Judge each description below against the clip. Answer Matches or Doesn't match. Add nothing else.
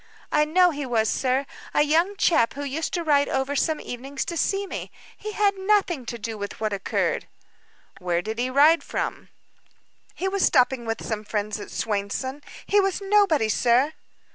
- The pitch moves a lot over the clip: Matches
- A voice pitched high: Matches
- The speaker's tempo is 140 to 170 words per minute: Doesn't match